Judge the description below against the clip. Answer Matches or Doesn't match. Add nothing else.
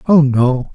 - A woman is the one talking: Doesn't match